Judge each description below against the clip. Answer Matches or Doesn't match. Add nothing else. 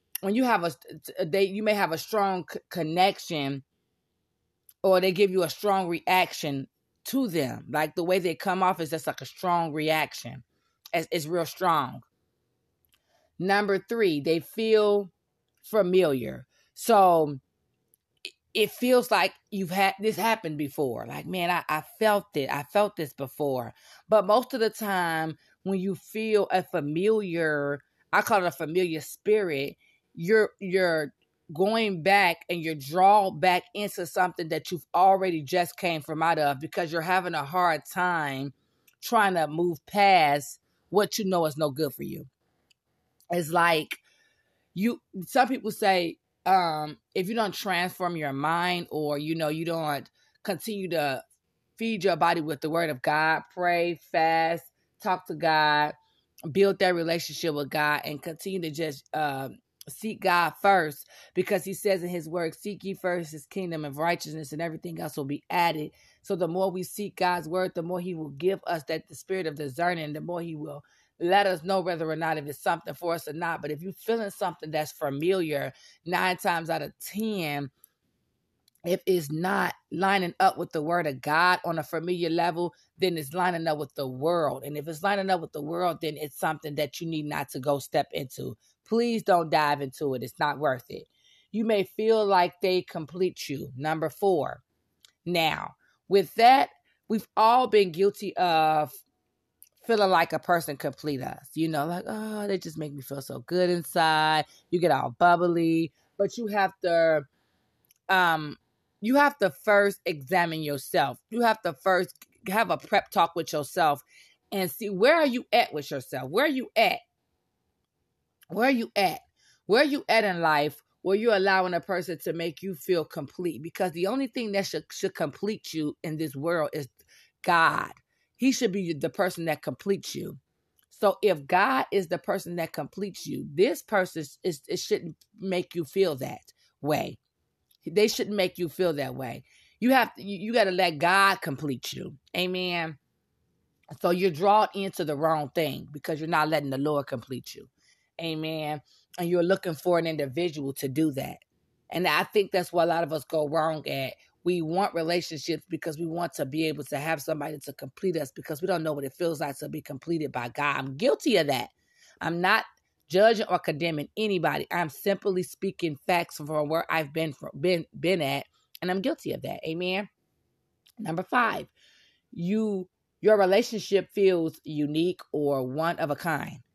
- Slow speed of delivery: Doesn't match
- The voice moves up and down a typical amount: Matches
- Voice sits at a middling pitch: Matches